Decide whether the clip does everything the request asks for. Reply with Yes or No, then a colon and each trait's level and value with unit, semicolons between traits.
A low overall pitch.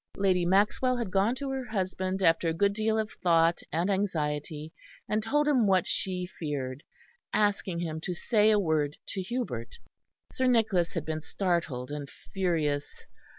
No: medium, 185 Hz